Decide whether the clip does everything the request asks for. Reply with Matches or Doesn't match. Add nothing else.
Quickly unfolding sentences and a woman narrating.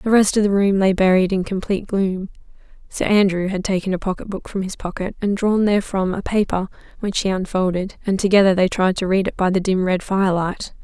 Matches